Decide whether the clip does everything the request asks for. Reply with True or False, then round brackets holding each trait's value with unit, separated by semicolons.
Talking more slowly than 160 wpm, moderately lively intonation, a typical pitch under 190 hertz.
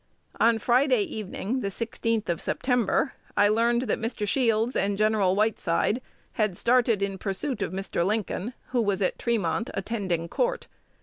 False (150 wpm; 3.2 semitones; 220 Hz)